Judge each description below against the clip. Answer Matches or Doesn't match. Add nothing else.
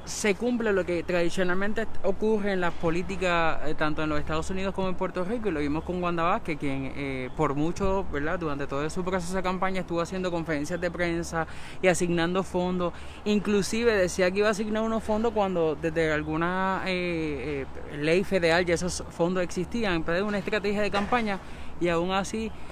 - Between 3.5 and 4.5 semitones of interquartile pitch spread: Doesn't match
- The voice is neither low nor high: Matches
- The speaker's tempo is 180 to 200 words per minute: Matches